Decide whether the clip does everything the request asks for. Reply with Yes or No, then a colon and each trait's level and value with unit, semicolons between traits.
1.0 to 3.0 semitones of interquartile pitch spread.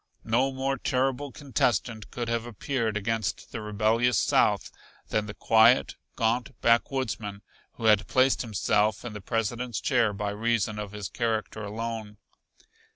Yes: narrow, 2.5 semitones